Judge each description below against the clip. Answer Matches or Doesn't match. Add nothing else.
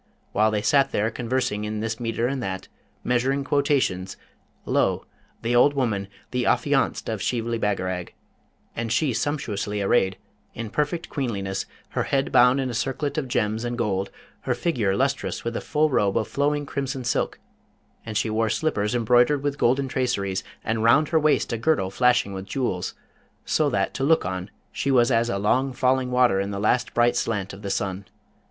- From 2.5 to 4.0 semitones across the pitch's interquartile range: Doesn't match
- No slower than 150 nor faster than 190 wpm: Matches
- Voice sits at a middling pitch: Doesn't match